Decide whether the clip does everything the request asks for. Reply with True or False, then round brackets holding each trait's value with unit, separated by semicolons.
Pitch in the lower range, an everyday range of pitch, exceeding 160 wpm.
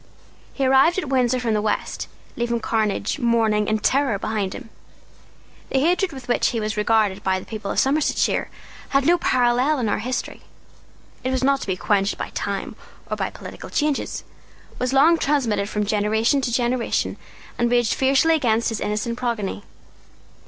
False (240 Hz; 3.9 semitones; 170 wpm)